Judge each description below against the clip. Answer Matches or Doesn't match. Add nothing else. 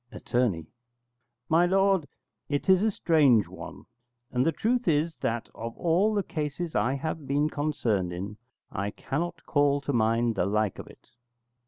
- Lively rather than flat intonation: Matches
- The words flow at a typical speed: Matches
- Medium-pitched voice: Matches